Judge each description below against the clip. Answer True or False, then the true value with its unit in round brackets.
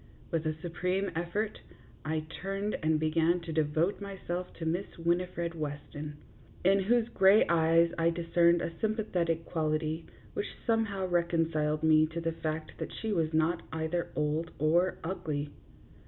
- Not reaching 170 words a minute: True (150 wpm)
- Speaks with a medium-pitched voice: True (165 Hz)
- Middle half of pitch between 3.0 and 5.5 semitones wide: False (2.5 semitones)